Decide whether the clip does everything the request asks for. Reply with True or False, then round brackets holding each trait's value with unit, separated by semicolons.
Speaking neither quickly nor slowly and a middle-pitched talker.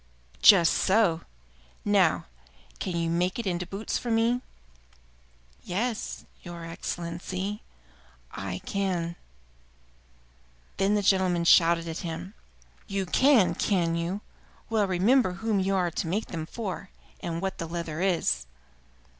False (125 wpm; 180 Hz)